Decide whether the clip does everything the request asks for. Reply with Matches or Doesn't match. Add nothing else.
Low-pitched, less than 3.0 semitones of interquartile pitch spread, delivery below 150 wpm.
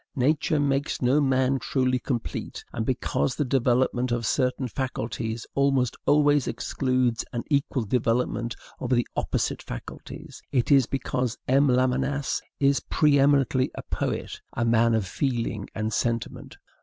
Matches